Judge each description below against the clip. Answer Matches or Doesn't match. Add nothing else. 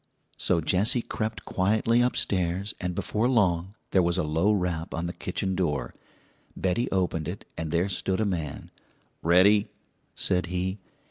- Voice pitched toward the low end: Matches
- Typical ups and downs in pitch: Matches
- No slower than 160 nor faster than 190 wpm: Doesn't match